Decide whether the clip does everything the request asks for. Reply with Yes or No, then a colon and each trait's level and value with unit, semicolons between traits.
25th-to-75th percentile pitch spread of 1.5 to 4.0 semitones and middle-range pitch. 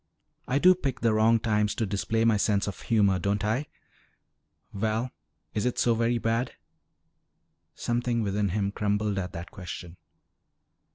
No: average, 2.7 semitones; low, 110 Hz